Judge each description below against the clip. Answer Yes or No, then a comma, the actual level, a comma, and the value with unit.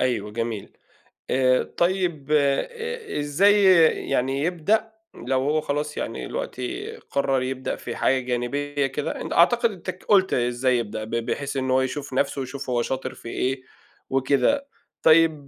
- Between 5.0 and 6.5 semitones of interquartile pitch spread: Yes, average, 5.3 semitones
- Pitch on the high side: No, medium, 140 Hz